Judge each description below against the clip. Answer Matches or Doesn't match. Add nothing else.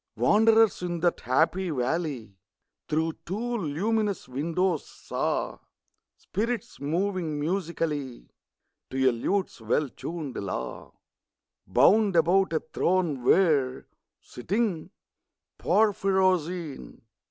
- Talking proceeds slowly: Matches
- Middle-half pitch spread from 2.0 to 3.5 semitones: Doesn't match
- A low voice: Doesn't match